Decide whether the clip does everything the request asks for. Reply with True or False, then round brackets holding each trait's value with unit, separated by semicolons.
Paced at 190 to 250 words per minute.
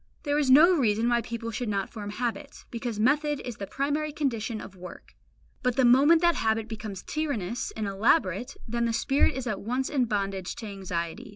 True (195 wpm)